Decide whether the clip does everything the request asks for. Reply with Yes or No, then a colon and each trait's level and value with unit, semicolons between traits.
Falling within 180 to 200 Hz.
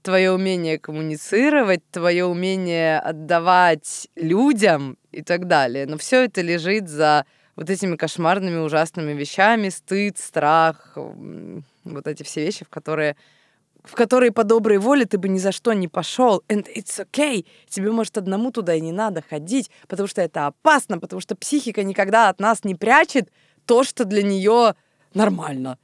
Yes: high, 190 Hz